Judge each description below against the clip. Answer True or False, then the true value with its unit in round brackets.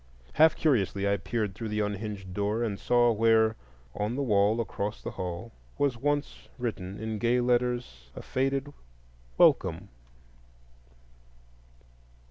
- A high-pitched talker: False (110 Hz)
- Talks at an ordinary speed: False (125 wpm)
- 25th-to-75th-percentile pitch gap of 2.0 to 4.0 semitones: True (3.3 semitones)